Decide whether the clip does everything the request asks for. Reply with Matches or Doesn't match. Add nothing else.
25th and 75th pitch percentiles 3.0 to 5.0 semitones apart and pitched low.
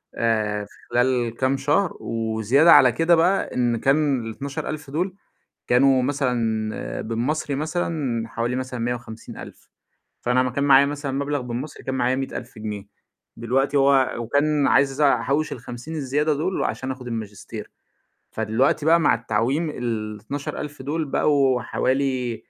Matches